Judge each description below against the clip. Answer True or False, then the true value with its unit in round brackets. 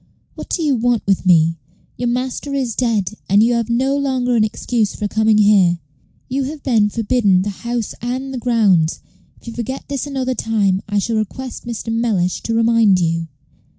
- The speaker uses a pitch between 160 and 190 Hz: False (230 Hz)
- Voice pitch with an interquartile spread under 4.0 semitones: True (3.5 semitones)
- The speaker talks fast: False (185 wpm)